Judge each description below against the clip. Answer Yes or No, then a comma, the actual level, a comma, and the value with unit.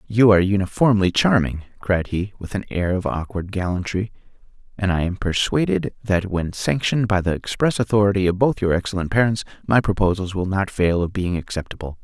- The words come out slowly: No, average, 180 wpm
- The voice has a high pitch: No, very low, 95 Hz